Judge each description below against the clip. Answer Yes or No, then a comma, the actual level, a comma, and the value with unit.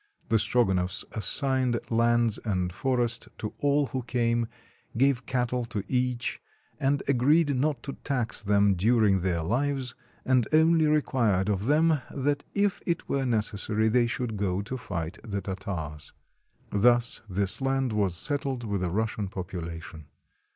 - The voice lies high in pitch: No, low, 115 Hz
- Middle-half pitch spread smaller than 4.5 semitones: No, average, 5.0 semitones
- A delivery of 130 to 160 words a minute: Yes, average, 145 wpm